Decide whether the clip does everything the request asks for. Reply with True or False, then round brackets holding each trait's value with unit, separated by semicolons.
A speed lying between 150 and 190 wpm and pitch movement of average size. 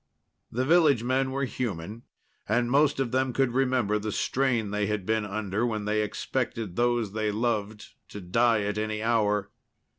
True (170 wpm; 3.4 semitones)